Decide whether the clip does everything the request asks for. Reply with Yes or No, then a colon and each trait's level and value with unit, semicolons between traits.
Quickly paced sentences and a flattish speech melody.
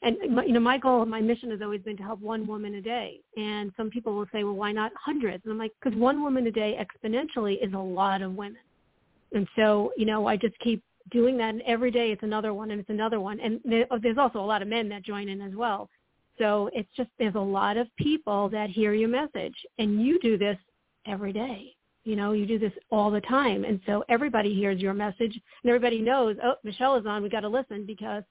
Yes: fast, 245 wpm; narrow, 2.3 semitones